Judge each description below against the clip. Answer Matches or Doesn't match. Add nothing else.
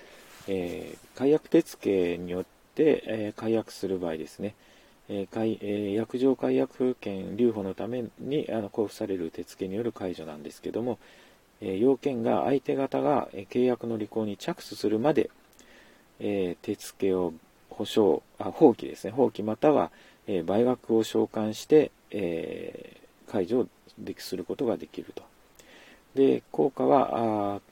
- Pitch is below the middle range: Matches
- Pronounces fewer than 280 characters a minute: Matches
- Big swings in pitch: Doesn't match